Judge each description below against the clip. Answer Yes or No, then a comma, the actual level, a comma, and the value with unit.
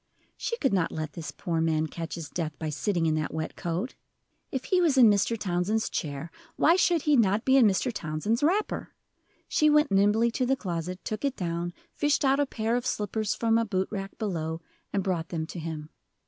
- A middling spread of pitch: No, wide, 6.9 semitones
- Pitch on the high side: Yes, high, 200 Hz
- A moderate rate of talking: No, fast, 210 wpm